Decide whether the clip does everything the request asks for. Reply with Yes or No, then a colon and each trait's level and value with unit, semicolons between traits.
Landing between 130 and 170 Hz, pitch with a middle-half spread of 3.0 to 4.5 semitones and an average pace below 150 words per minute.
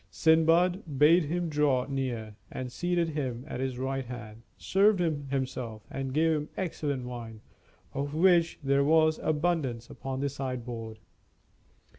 Yes: medium, 140 Hz; average, 4.2 semitones; average, 140 wpm